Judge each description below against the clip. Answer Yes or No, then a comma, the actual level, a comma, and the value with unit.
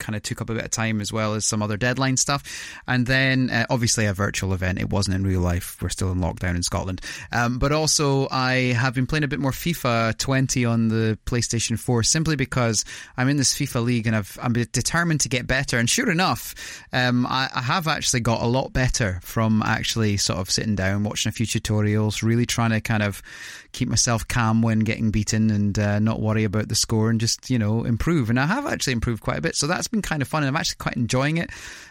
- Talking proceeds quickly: Yes, fast, 240 wpm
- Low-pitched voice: Yes, low, 115 Hz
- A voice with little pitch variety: No, average, 3.1 semitones